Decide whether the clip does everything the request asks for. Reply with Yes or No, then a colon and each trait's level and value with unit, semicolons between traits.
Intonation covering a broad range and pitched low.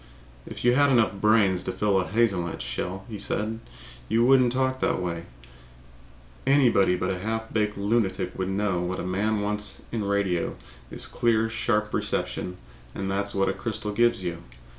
No: average, 3.2 semitones; low, 105 Hz